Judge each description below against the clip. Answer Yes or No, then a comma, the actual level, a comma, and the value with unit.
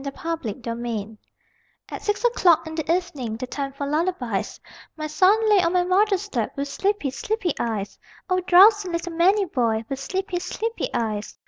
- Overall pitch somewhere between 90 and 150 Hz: No, very high, 330 Hz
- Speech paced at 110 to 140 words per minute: No, average, 170 wpm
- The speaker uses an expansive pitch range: Yes, wide, 7.2 semitones